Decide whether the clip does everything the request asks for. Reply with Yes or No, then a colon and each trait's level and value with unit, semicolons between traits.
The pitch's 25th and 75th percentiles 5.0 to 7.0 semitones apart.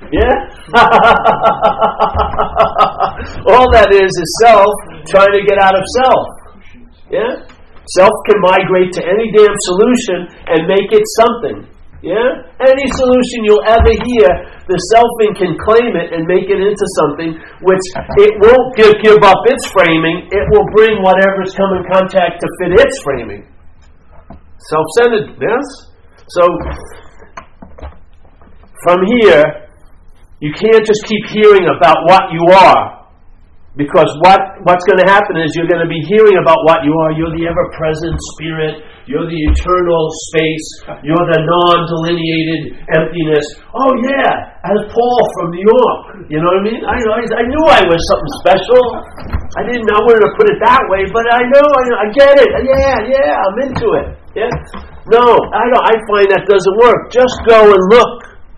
Yes: average, 5.3 semitones